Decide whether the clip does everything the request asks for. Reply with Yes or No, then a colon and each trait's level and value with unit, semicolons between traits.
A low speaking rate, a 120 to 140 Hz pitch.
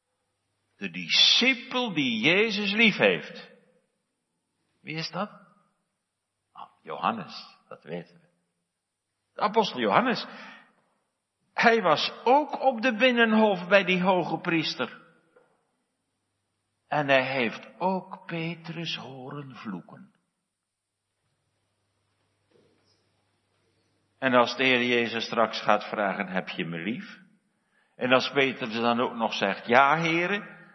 Yes: slow, 105 wpm; low, 135 Hz